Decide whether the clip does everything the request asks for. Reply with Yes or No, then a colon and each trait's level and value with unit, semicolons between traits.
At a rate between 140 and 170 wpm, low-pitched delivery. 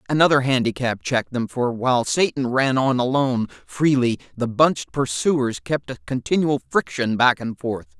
Yes: average, 160 wpm; low, 125 Hz